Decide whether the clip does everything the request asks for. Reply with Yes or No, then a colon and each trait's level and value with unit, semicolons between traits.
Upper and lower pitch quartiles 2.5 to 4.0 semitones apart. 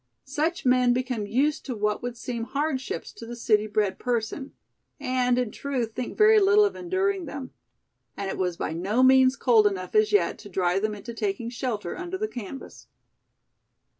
No: average, 4.5 semitones